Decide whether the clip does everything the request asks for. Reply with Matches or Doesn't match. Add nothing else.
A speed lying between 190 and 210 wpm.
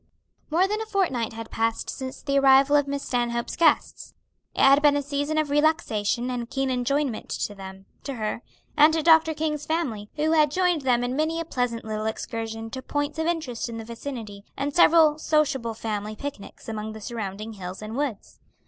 Matches